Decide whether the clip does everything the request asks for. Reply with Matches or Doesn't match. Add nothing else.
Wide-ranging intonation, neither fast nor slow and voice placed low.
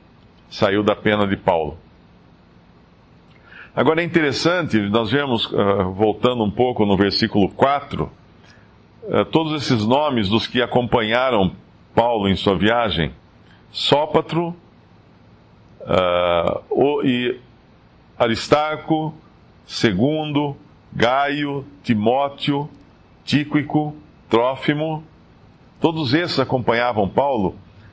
Doesn't match